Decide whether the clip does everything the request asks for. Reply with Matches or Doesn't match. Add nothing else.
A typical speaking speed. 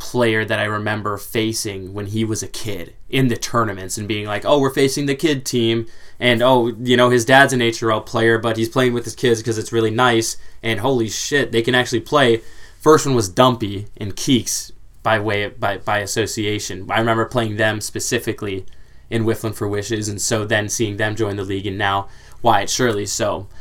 Doesn't match